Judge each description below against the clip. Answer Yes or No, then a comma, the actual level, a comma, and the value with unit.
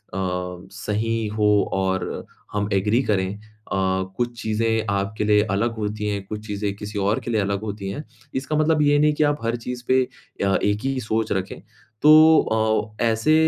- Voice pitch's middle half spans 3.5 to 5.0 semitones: No, average, 2.9 semitones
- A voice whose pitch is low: Yes, low, 105 Hz